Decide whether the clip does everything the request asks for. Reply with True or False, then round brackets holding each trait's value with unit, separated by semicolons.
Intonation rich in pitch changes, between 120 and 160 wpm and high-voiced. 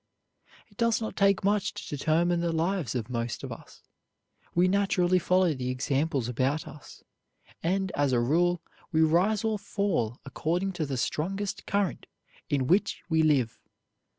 False (5.8 semitones; 155 wpm; 170 Hz)